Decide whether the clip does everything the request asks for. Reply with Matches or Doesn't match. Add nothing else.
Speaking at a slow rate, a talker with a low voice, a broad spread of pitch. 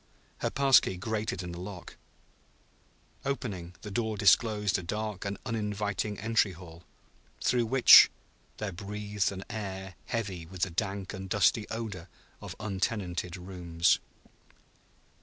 Doesn't match